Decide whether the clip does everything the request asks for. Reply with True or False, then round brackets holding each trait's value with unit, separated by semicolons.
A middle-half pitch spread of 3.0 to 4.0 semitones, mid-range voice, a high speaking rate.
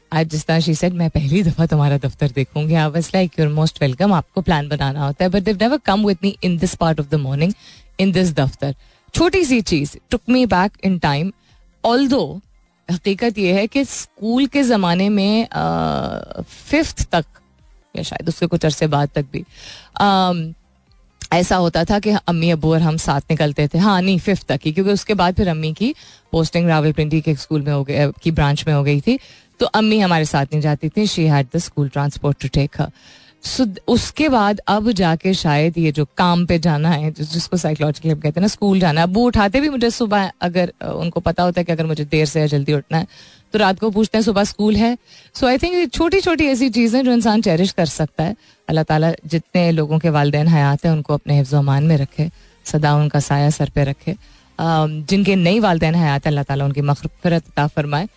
False (4.8 semitones; 165 Hz; 205 wpm)